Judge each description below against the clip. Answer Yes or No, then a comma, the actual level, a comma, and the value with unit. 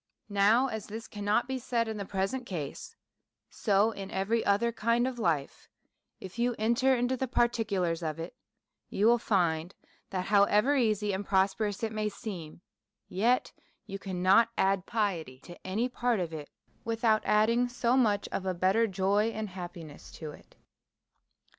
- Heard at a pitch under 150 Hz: No, high, 210 Hz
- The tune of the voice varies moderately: Yes, average, 3.6 semitones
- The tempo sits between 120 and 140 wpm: No, average, 165 wpm